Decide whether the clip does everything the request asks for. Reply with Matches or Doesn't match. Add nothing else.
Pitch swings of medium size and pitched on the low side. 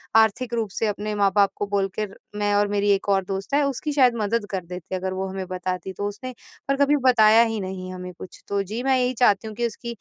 Doesn't match